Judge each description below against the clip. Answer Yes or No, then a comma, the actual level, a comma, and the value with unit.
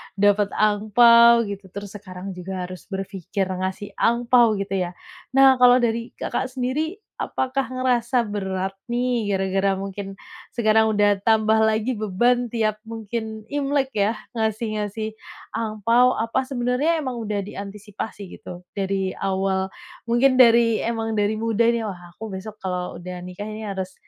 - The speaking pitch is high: Yes, high, 215 Hz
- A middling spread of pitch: Yes, average, 3.3 semitones